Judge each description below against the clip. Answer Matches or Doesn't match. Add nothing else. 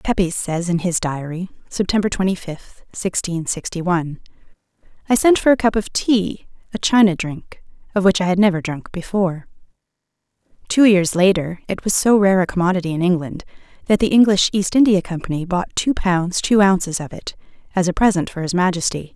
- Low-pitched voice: Doesn't match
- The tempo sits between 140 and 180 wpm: Matches